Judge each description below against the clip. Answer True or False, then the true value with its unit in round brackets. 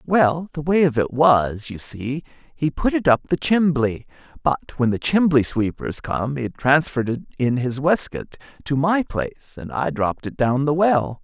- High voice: False (140 Hz)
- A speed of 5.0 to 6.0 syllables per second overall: False (4.4 syllables/s)